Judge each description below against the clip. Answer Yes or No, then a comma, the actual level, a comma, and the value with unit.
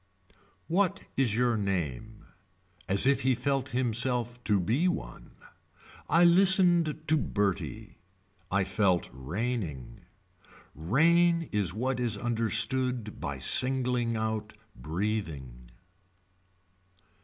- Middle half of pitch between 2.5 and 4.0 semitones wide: No, average, 5.2 semitones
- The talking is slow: Yes, slow, 95 wpm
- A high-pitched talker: No, low, 115 Hz